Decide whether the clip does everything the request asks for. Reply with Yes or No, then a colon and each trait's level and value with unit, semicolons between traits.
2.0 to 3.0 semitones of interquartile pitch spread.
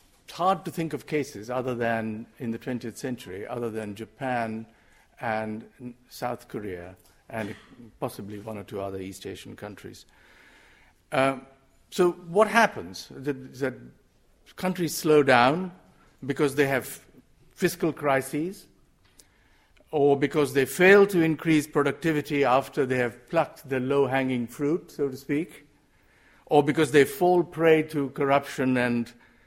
No: average, 4.2 semitones